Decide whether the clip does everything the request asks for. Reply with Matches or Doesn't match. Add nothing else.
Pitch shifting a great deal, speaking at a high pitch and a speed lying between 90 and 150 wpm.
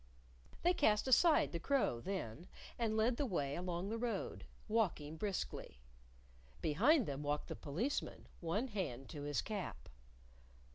Matches